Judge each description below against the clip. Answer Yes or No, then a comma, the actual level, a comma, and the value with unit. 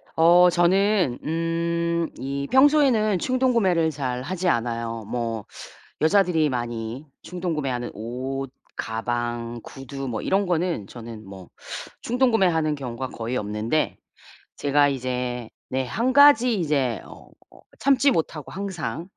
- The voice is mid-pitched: Yes, medium, 145 Hz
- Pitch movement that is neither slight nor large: No, wide, 7.2 semitones